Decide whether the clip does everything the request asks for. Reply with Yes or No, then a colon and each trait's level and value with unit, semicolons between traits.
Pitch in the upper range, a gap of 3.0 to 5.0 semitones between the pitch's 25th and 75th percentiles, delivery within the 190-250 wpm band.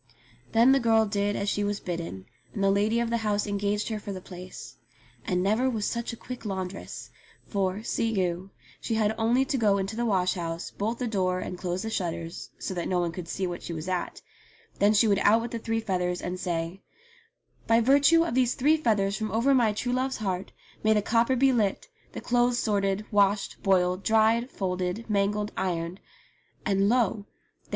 Yes: high, 205 Hz; average, 3.7 semitones; average, 200 wpm